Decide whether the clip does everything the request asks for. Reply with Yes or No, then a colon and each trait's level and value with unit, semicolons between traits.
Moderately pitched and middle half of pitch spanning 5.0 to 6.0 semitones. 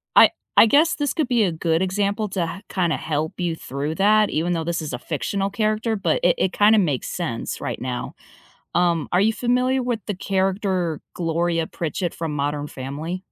No: medium, 180 Hz; average, 4.6 semitones